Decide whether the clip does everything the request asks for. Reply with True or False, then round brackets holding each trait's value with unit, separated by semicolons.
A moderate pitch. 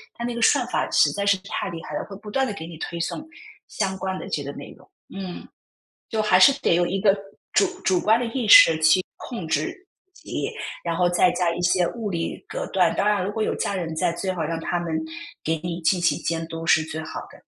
True (180 Hz)